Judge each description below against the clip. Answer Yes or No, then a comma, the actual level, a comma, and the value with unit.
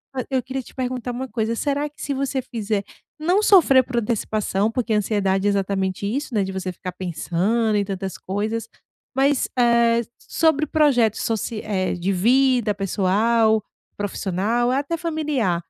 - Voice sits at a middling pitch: No, high, 225 Hz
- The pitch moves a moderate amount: Yes, average, 4.8 semitones